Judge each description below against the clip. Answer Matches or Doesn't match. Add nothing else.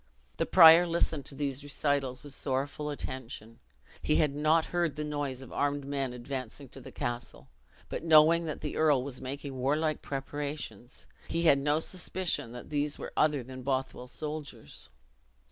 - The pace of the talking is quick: Doesn't match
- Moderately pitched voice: Matches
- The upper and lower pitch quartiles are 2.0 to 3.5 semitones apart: Matches